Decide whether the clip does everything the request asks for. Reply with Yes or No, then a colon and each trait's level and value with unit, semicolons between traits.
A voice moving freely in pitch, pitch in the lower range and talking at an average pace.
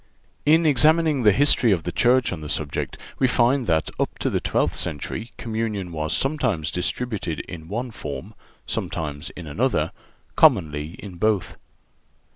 Yes: wide, 7.4 semitones; low, 105 Hz; average, 150 wpm